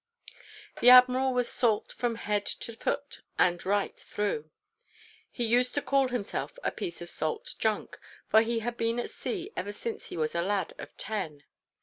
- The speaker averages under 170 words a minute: No, average, 180 wpm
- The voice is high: Yes, high, 230 Hz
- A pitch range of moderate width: Yes, average, 3.7 semitones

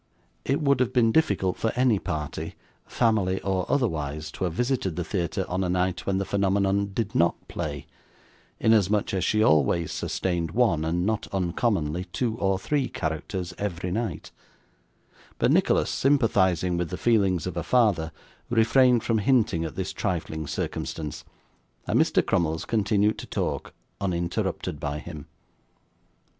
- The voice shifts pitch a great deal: No, average, 4.6 semitones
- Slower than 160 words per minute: Yes, average, 150 wpm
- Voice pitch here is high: No, very low, 95 Hz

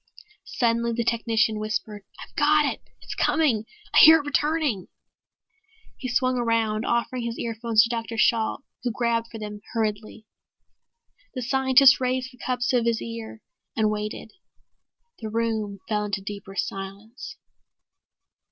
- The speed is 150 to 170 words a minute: No, average, 140 wpm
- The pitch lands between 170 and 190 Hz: No, high, 230 Hz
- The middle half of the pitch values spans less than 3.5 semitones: Yes, average, 2.7 semitones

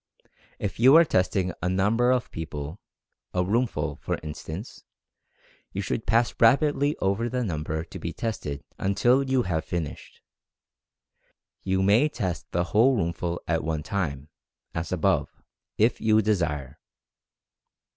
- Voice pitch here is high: No, very low, 95 Hz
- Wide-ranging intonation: Yes, wide, 6.2 semitones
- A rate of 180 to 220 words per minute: No, slow, 135 wpm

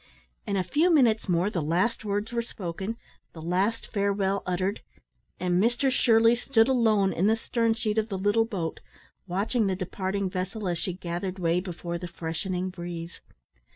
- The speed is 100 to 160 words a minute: No, average, 170 wpm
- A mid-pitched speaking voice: No, high, 195 Hz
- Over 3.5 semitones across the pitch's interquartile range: Yes, average, 3.9 semitones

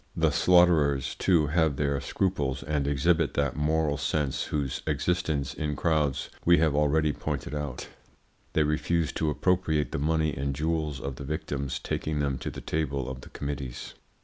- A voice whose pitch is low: Yes, very low, 75 Hz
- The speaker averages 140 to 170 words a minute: Yes, average, 165 wpm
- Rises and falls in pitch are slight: Yes, narrow, 2.1 semitones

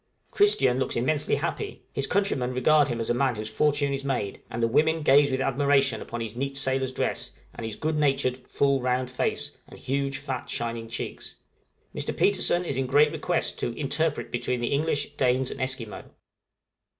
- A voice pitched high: No, low, 135 Hz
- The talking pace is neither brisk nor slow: Yes, average, 185 wpm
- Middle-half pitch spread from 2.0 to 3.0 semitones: Yes, narrow, 2.5 semitones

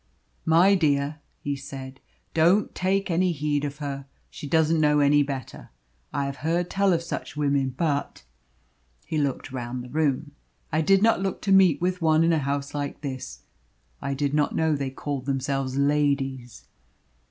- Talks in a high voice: No, medium, 145 Hz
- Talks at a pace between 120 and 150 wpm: No, average, 170 wpm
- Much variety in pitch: No, average, 2.9 semitones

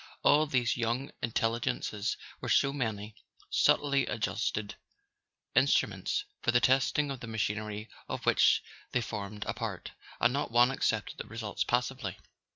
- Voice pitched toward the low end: Yes, low, 115 Hz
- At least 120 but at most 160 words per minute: Yes, average, 145 wpm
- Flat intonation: No, average, 3.7 semitones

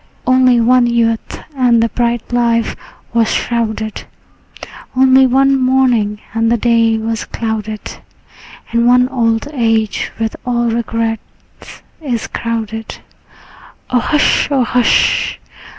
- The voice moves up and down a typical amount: No, narrow, 1.8 semitones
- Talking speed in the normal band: No, slow, 115 wpm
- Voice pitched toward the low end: No, high, 235 Hz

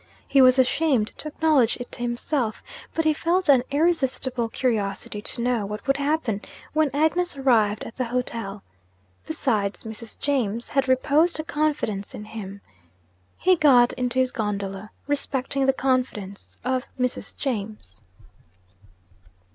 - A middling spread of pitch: Yes, average, 4.7 semitones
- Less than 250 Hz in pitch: No, very high, 255 Hz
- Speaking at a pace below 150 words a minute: Yes, average, 140 wpm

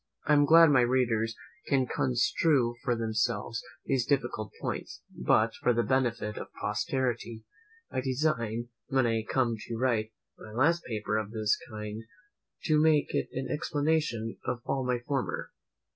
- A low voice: Yes, low, 120 Hz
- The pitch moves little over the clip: No, average, 3.3 semitones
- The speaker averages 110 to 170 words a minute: Yes, average, 150 wpm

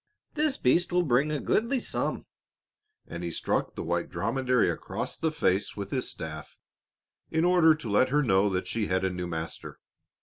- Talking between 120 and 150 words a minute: No, average, 180 wpm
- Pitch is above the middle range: No, low, 120 Hz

